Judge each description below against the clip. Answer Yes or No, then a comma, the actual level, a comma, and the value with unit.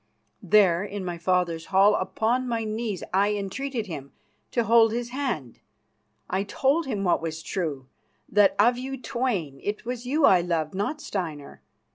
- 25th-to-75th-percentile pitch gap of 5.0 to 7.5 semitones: Yes, average, 5.3 semitones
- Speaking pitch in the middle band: No, high, 205 Hz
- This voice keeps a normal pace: Yes, average, 160 wpm